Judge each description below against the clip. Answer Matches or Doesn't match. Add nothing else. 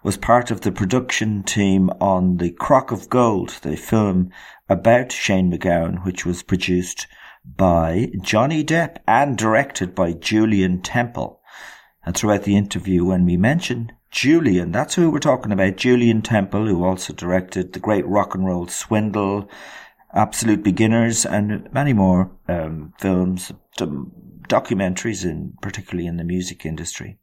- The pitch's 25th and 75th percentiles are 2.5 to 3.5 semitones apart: Matches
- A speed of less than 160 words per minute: Matches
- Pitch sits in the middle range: Doesn't match